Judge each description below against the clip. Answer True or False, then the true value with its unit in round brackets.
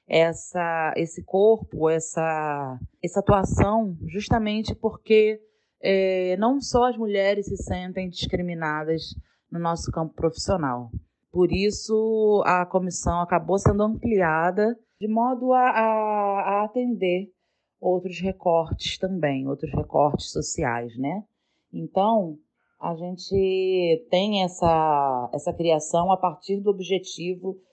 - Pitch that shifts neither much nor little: True (4.1 semitones)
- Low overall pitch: False (185 Hz)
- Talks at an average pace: False (110 wpm)